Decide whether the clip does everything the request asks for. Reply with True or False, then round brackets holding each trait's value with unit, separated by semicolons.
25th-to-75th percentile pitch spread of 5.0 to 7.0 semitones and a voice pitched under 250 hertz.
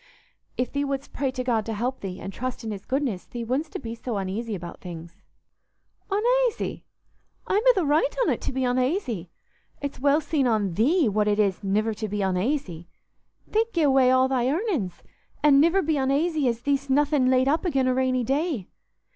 False (5.3 semitones; 255 Hz)